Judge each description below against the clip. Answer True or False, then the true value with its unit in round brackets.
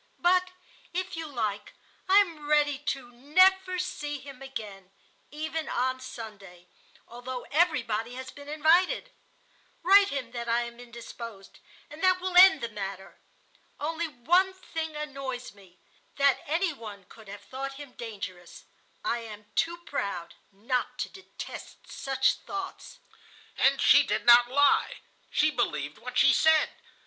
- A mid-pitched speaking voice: False (270 Hz)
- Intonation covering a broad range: True (5.7 semitones)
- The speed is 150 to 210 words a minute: False (140 wpm)